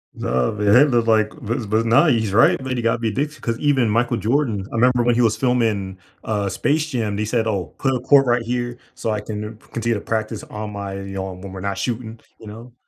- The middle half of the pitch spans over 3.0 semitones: No, average, 2.7 semitones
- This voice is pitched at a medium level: No, low, 115 Hz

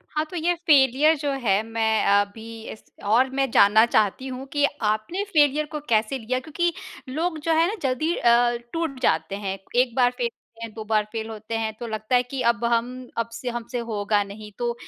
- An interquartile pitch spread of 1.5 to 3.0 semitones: No, average, 4.3 semitones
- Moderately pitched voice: No, high, 240 Hz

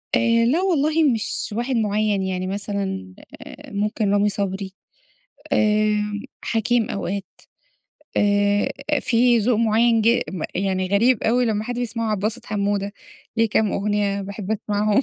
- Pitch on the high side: Yes, high, 210 Hz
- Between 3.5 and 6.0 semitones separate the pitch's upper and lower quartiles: No, narrow, 2.4 semitones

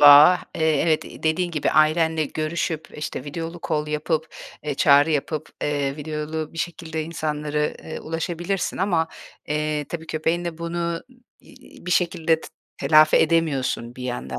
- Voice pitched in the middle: Yes, medium, 155 Hz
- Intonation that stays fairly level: Yes, narrow, 1.7 semitones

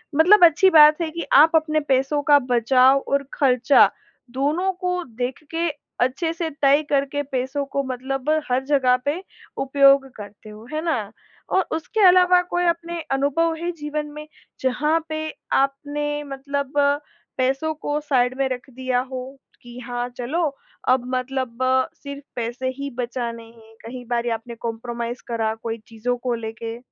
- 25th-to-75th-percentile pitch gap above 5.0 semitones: No, average, 3.6 semitones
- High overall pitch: Yes, very high, 270 Hz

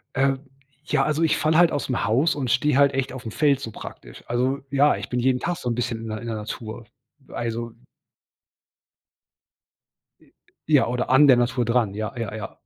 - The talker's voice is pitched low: Yes, low, 125 Hz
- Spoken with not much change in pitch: No, average, 3.2 semitones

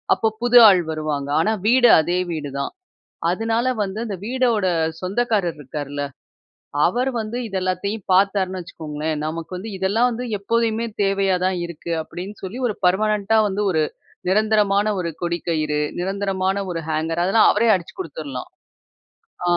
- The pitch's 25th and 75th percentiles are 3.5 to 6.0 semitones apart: Yes, average, 4.4 semitones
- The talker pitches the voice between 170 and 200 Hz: Yes, high, 190 Hz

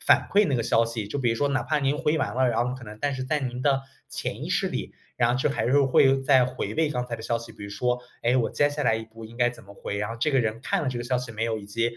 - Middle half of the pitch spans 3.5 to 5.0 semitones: No, average, 2.9 semitones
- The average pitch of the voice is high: No, low, 125 Hz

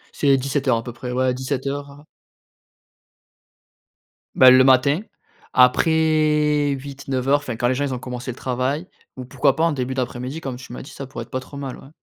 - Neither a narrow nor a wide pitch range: No, narrow, 2.1 semitones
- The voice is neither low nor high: No, low, 130 Hz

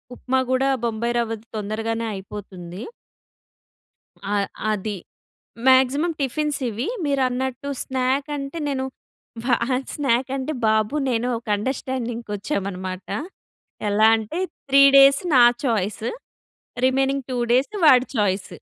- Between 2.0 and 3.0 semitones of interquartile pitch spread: No, average, 4.0 semitones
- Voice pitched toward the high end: Yes, high, 245 Hz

